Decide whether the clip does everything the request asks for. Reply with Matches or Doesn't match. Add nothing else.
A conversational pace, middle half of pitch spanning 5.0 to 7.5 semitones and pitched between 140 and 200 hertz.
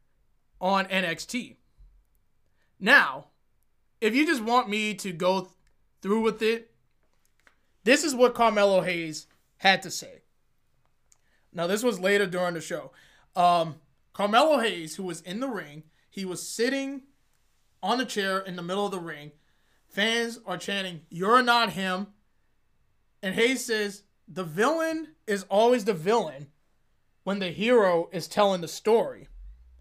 Matches